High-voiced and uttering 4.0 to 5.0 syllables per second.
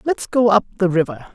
No: high, 200 Hz; 5.6 syllables/s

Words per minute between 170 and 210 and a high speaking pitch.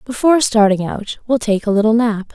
Yes: fast, 205 wpm; high, 220 Hz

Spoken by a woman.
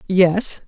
Yes: female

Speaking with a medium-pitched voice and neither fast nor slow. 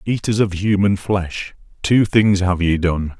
No: very low, 95 Hz; average, 170 wpm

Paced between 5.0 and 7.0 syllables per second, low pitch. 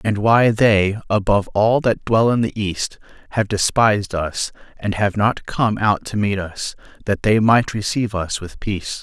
No: 4.5 syllables/s; low, 105 Hz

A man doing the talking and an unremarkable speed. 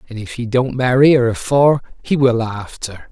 Yes: male; average, 195 wpm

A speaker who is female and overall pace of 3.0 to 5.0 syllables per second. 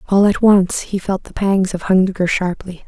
Yes: female; 4.5 syllables/s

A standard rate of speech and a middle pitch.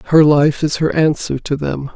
No: fast, 215 wpm; medium, 150 Hz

